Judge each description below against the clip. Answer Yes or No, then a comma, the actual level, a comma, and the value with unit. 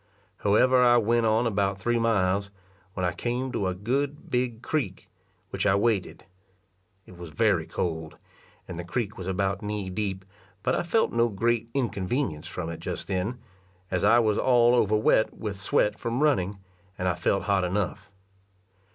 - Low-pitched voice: Yes, low, 105 Hz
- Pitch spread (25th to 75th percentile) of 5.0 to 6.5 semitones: No, average, 4.1 semitones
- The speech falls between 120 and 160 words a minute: No, average, 170 wpm